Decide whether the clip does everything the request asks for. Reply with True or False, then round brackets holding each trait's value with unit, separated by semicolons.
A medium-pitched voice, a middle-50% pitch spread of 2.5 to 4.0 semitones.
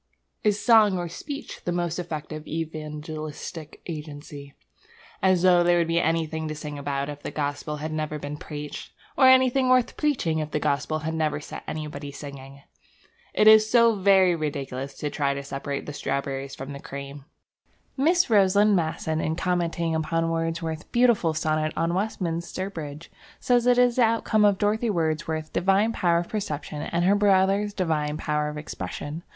False (160 Hz; 4.5 semitones)